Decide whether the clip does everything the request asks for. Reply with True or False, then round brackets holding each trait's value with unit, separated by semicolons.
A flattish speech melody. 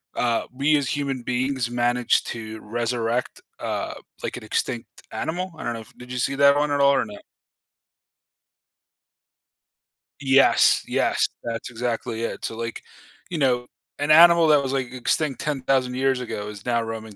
False (3.1 semitones)